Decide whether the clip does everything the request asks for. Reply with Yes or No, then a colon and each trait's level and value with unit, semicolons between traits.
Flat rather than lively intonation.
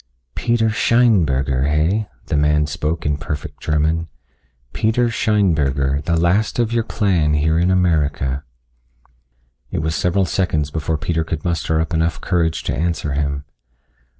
No: average, 3.7 semitones